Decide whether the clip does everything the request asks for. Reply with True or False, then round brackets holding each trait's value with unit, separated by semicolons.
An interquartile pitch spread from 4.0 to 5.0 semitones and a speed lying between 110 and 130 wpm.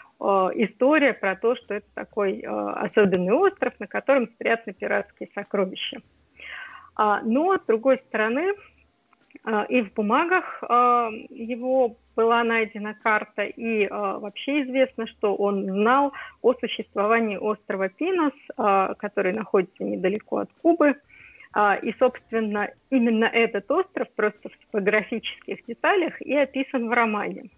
True (4.4 semitones; 115 wpm)